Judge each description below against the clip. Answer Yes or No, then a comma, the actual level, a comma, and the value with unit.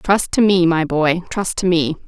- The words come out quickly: Yes, fast, 230 wpm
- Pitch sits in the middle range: Yes, medium, 175 Hz